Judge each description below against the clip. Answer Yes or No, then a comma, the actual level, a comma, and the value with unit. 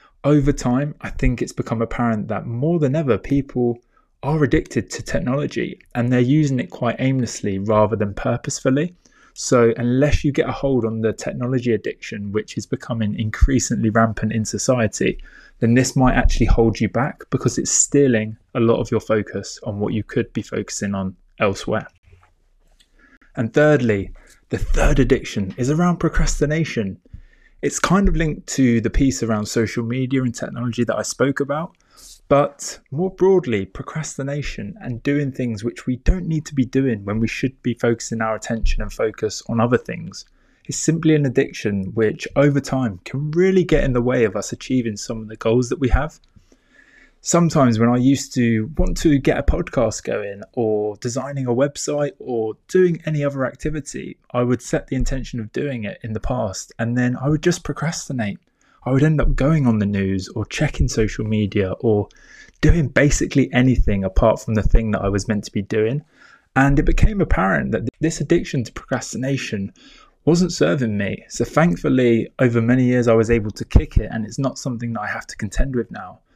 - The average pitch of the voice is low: Yes, low, 125 Hz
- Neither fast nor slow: Yes, average, 185 wpm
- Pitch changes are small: No, average, 4.2 semitones